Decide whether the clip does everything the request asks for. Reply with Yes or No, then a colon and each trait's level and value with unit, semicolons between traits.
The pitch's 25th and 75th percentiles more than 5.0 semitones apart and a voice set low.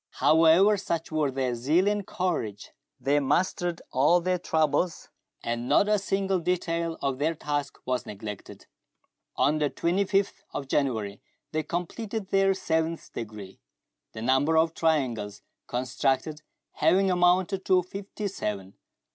No: wide, 5.6 semitones; medium, 160 Hz